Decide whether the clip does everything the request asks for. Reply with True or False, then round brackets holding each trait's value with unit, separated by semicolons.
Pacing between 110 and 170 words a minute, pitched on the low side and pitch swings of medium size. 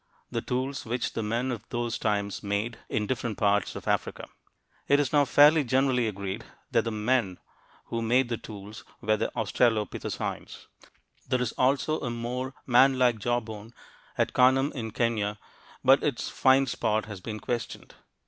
True (160 wpm; 120 Hz; 3.1 semitones)